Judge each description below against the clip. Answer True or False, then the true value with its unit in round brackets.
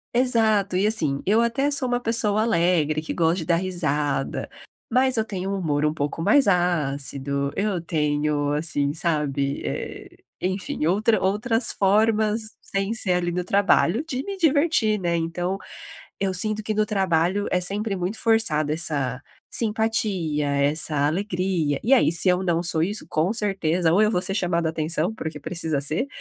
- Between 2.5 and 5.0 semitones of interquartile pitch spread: False (5.4 semitones)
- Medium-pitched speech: True (180 Hz)